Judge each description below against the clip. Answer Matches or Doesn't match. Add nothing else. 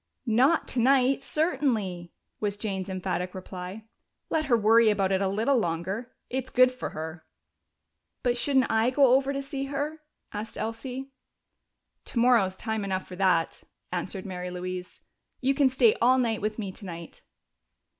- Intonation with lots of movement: Matches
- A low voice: Doesn't match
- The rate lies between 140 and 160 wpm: Matches